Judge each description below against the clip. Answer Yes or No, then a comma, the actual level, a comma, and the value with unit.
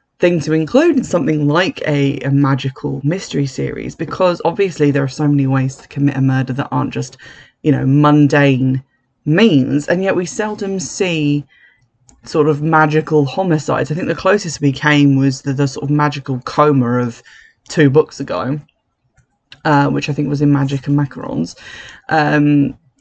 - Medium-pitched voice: Yes, medium, 145 Hz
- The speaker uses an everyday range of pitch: No, narrow, 2.3 semitones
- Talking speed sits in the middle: Yes, average, 170 wpm